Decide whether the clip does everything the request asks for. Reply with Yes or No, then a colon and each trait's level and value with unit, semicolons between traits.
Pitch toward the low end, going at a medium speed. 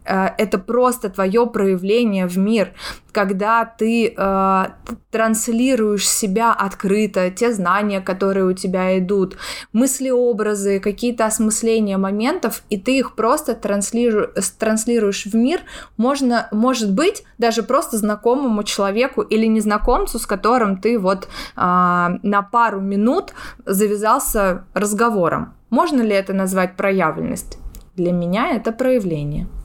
No: high, 215 Hz; average, 120 wpm